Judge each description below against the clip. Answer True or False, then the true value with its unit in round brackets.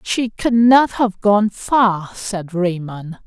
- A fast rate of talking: False (145 wpm)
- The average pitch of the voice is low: False (205 Hz)